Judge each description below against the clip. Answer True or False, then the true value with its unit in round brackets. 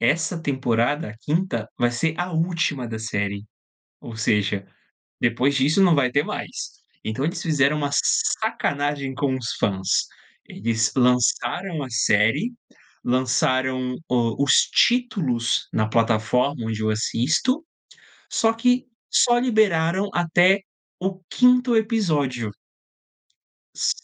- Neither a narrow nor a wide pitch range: False (7.0 semitones)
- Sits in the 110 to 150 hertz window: True (135 Hz)